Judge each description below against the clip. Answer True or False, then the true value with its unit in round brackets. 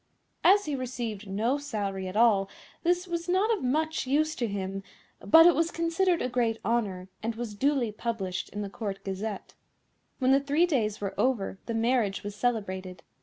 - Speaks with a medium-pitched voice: False (235 Hz)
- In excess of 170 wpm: True (180 wpm)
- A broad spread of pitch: True (6.4 semitones)